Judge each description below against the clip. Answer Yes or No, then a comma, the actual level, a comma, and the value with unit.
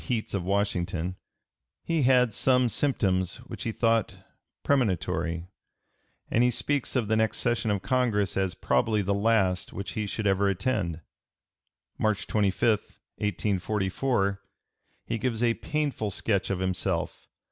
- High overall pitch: No, low, 105 Hz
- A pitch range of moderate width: Yes, average, 4.0 semitones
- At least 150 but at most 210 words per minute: No, slow, 135 wpm